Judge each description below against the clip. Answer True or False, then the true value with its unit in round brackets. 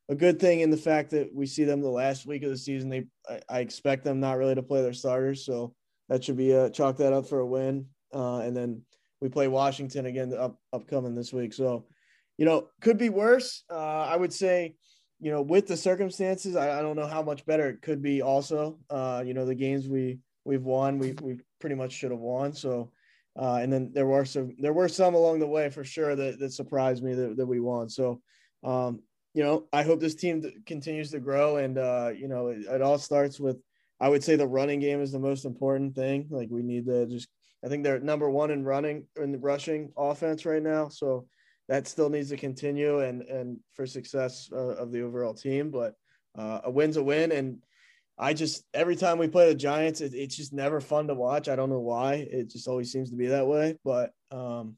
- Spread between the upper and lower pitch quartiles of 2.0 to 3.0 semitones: True (2.7 semitones)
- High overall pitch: False (135 Hz)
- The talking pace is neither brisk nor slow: False (235 wpm)